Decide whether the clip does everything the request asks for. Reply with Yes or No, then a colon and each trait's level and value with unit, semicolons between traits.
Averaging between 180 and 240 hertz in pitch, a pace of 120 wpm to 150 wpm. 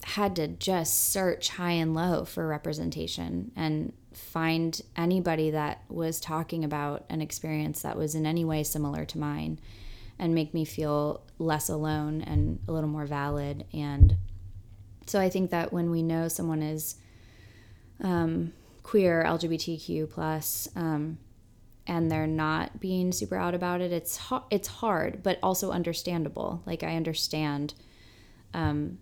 No: medium, 155 Hz; average, 145 wpm